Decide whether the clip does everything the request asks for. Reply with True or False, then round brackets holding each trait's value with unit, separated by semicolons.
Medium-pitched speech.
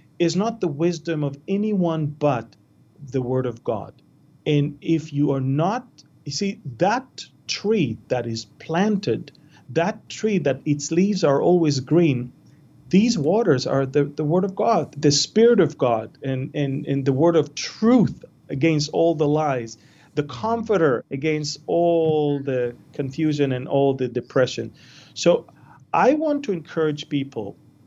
True (150 Hz)